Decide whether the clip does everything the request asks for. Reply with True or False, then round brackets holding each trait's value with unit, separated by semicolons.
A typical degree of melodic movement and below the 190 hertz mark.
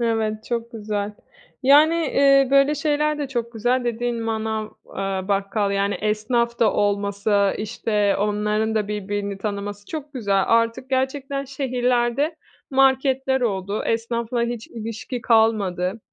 False (3.9 semitones; 230 Hz)